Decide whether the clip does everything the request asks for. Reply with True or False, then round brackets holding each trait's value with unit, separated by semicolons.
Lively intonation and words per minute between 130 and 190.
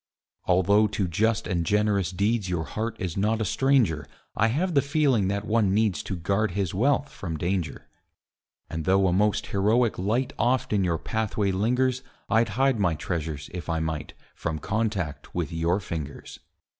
False (4.3 semitones; 170 wpm)